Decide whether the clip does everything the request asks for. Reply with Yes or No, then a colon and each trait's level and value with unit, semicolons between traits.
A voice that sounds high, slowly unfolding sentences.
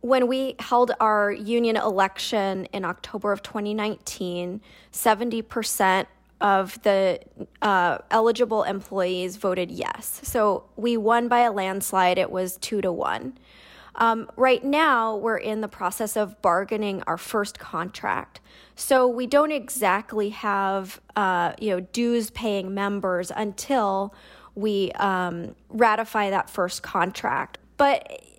Yes: high, 210 Hz; slow, 125 wpm